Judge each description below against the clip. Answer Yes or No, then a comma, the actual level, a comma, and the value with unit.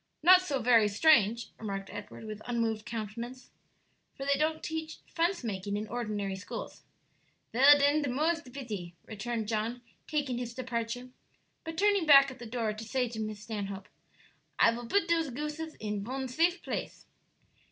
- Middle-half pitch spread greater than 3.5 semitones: Yes, wide, 5.6 semitones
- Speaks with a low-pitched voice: No, high, 245 Hz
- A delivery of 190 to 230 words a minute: No, average, 170 wpm